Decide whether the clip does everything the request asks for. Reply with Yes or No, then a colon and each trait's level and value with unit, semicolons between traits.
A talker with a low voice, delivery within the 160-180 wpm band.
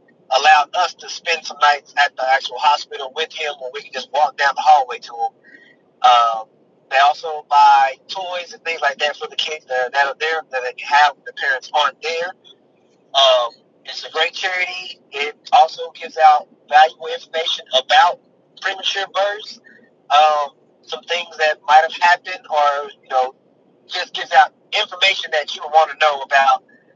No: medium, 160 Hz; average, 175 wpm